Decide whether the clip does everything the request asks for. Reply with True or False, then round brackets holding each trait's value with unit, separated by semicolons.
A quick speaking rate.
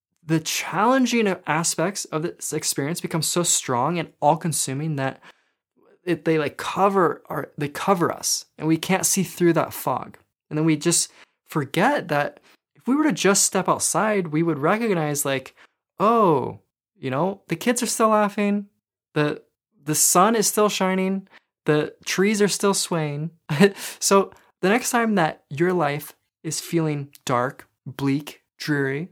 False (155 wpm)